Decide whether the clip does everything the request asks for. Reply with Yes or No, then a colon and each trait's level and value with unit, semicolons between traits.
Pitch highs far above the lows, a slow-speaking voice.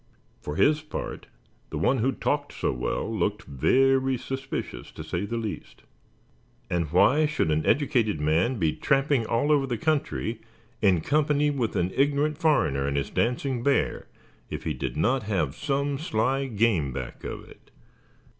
No: wide, 7.2 semitones; average, 160 wpm